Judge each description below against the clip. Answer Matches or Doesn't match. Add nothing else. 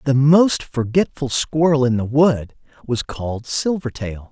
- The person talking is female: Doesn't match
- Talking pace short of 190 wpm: Matches